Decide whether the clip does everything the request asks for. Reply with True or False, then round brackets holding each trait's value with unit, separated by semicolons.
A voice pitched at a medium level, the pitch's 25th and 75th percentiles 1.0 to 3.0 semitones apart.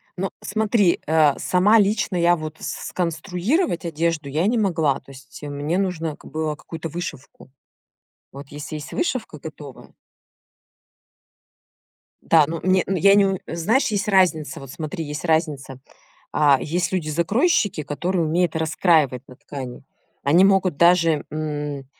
False (165 Hz; 4.0 semitones)